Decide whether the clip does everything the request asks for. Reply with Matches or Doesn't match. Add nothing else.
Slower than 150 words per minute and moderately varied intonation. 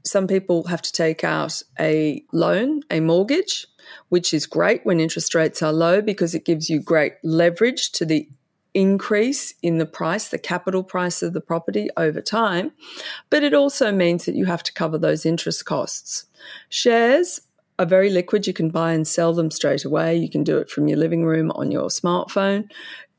Doesn't match